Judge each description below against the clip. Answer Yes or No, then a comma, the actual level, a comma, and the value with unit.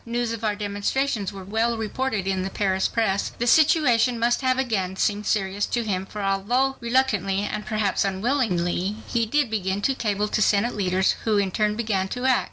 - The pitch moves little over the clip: No, average, 3.5 semitones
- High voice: Yes, high, 210 Hz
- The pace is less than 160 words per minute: No, average, 190 wpm